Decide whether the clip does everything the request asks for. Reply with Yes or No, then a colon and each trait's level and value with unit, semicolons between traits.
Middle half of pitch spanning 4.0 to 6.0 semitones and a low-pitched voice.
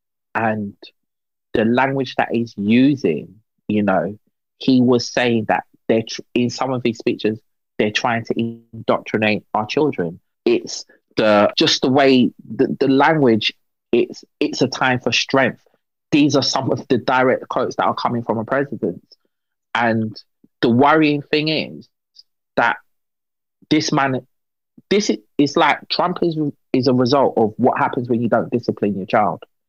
No: average, 3.4 semitones; low, 125 Hz